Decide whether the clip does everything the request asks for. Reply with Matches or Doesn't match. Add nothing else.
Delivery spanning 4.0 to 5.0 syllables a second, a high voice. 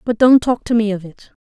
Doesn't match